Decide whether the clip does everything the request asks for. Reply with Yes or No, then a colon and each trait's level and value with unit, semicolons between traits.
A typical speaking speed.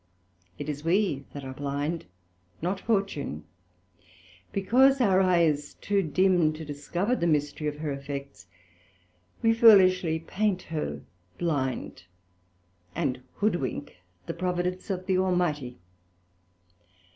No: slow, 115 wpm